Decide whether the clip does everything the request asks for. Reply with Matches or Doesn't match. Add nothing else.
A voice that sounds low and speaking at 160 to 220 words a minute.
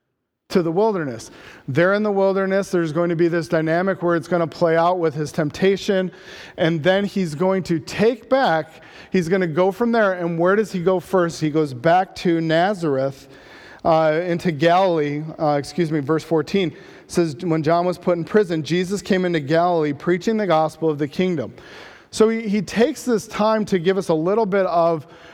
Doesn't match